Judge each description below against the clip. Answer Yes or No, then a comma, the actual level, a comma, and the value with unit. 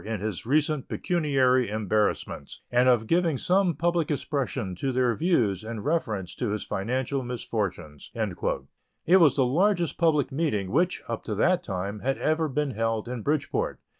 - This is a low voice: Yes, low, 130 Hz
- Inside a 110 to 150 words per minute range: No, average, 160 wpm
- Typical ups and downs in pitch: No, wide, 6.2 semitones